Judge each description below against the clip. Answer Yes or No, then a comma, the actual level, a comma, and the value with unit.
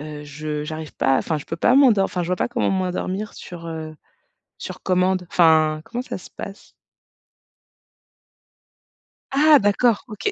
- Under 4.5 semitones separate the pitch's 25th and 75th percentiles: No, average, 4.9 semitones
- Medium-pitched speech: Yes, medium, 180 Hz